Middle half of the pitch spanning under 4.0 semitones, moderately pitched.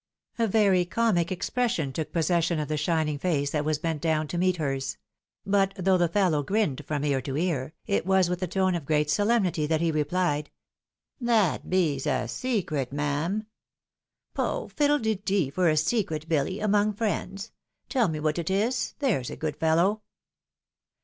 No: average, 4.7 semitones; medium, 175 Hz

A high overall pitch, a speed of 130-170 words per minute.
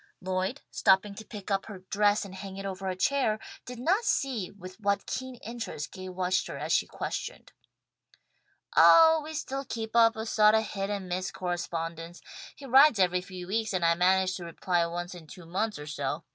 No: high, 195 Hz; average, 200 wpm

